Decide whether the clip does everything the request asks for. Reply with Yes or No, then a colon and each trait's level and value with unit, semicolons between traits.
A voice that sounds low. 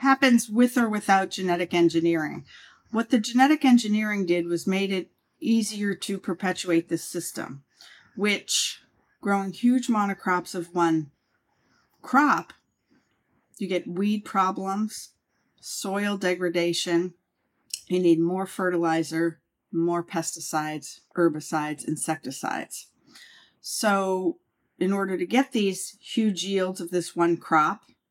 No: medium, 185 Hz